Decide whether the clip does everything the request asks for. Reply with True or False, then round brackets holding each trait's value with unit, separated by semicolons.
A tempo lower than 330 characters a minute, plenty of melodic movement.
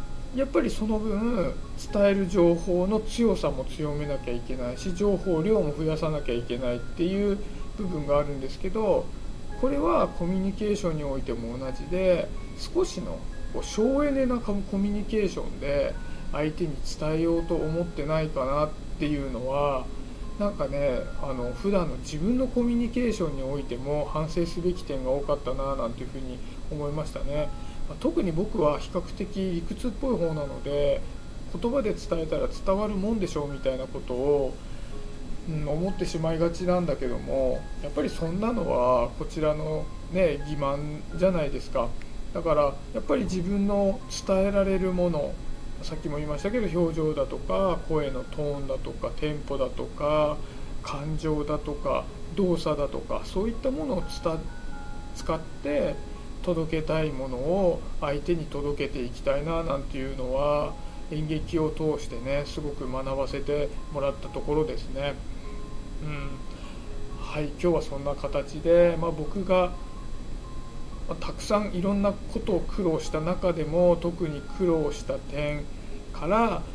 False (320 characters per minute; 4.8 semitones)